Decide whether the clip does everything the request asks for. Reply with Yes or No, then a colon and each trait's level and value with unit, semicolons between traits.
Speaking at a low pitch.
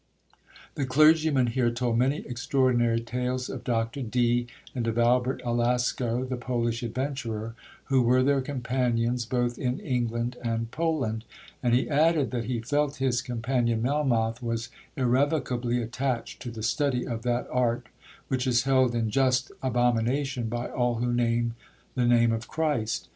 Yes: low, 125 Hz